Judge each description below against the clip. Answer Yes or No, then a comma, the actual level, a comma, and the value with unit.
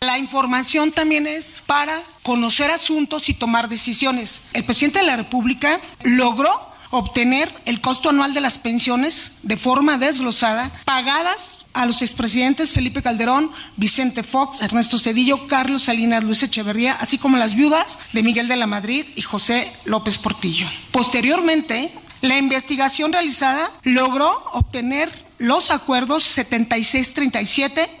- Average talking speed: Yes, average, 135 wpm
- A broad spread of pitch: No, average, 3.9 semitones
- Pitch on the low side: No, very high, 260 Hz